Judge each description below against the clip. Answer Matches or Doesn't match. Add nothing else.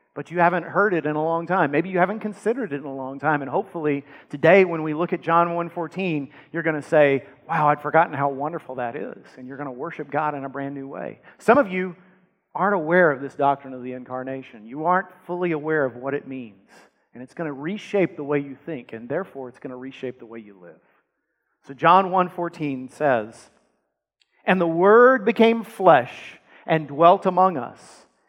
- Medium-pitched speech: Matches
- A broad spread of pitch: Doesn't match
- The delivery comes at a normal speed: Doesn't match